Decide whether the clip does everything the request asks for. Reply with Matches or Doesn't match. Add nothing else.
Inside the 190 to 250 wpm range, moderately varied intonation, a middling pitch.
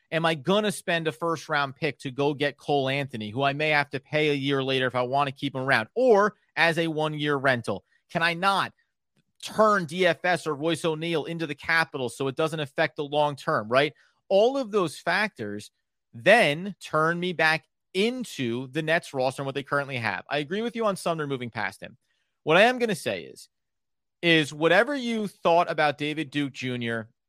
Matches